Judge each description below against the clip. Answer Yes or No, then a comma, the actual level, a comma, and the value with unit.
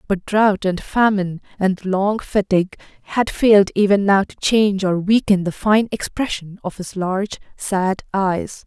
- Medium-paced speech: Yes, average, 160 wpm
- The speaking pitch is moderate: No, high, 195 Hz